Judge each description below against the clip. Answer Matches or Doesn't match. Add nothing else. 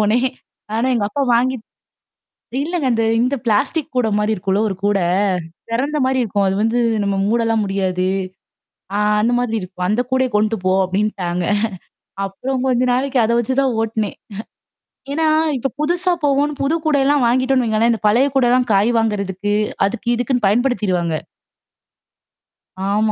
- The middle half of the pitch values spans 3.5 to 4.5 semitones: Matches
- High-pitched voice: Matches